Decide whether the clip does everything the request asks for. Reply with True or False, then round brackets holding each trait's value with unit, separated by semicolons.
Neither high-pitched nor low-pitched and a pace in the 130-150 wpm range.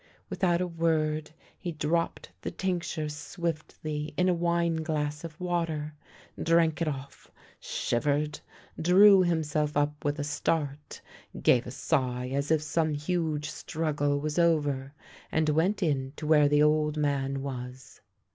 True (150 Hz; 140 wpm)